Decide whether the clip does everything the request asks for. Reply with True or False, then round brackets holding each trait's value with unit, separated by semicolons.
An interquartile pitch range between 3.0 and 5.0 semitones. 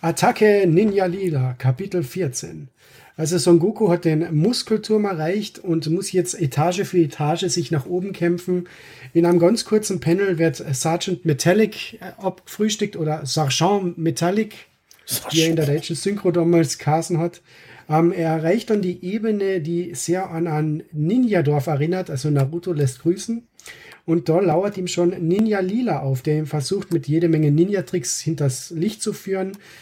True (3.3 semitones)